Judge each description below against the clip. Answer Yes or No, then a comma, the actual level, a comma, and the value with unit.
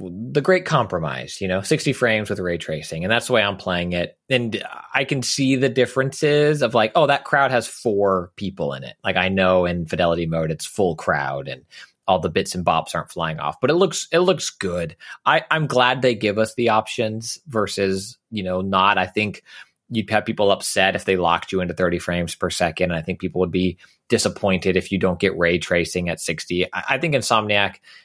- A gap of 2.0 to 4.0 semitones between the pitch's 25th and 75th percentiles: No, wide, 5.5 semitones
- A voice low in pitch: Yes, low, 100 Hz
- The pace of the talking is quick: Yes, fast, 220 wpm